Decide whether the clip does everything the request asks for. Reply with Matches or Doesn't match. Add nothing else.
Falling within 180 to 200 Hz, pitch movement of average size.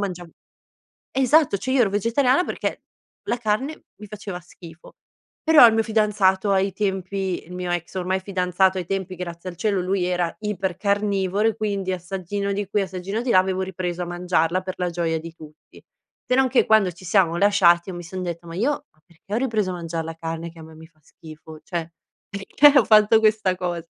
Matches